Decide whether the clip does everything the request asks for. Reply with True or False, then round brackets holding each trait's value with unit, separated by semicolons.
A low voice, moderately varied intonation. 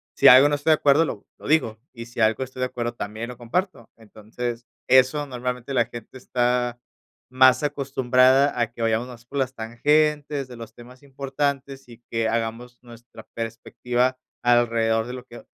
False (125 Hz; 2.3 semitones)